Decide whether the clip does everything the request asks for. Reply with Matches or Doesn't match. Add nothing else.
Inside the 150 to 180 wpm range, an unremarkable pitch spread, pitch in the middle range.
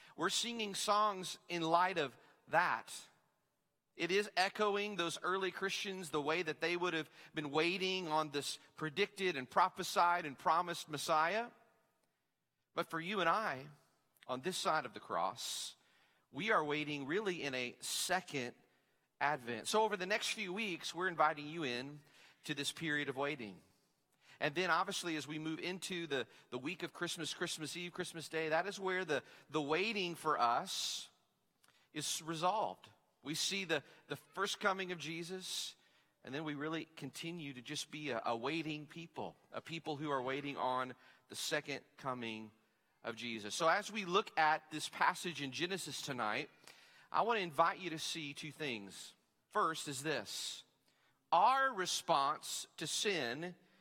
Matches